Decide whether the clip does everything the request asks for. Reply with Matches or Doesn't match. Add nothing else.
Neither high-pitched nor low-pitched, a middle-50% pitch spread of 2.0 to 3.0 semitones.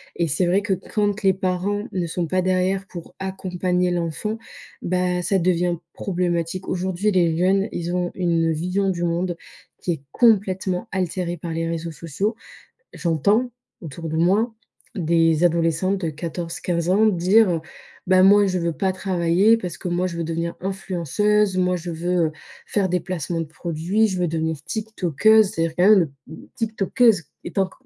Matches